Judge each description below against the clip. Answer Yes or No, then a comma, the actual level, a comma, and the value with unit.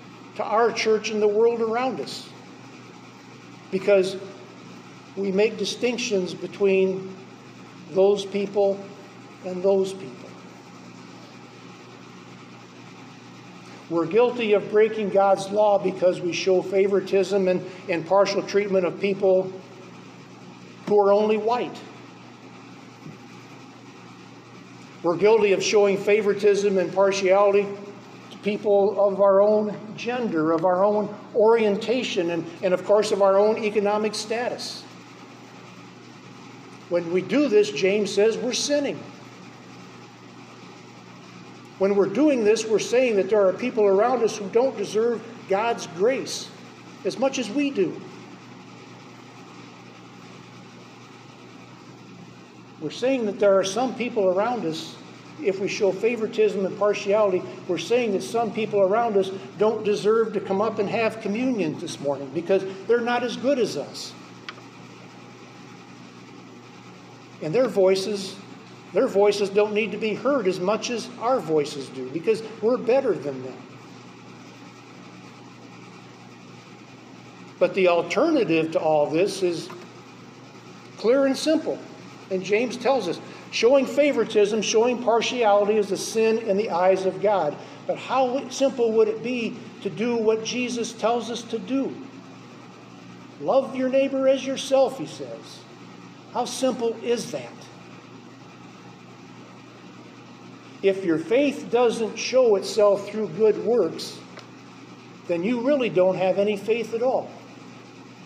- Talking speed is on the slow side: Yes, slow, 125 wpm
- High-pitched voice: Yes, high, 200 Hz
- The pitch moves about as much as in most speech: Yes, average, 4.6 semitones